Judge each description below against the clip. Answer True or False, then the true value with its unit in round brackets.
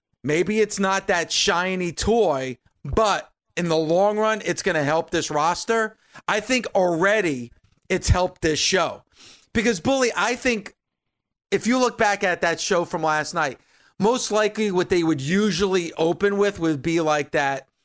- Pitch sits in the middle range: True (180 Hz)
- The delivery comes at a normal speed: True (170 wpm)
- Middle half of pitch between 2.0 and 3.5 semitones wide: False (4.7 semitones)